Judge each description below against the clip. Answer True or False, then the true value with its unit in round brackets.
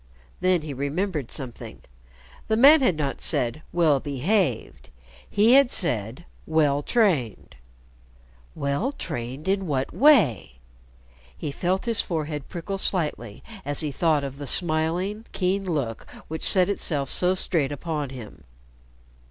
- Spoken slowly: True (130 wpm)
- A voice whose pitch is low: False (155 Hz)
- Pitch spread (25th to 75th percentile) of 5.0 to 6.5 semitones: True (5.3 semitones)